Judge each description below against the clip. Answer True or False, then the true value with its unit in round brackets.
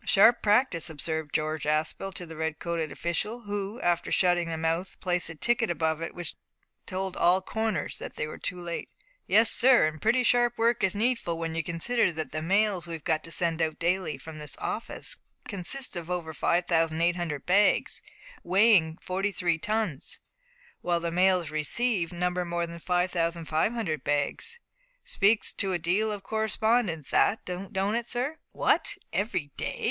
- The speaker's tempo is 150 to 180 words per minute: True (165 wpm)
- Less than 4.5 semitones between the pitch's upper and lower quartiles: True (4.1 semitones)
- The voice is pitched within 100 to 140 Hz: False (175 Hz)